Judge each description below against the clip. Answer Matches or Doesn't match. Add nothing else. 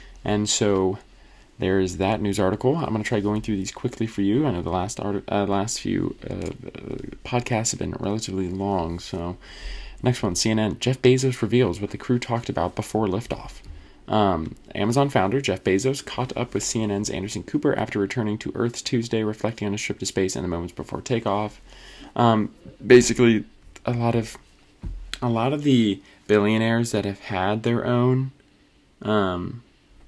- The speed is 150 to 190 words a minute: Matches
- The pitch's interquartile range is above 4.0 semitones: Doesn't match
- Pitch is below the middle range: Matches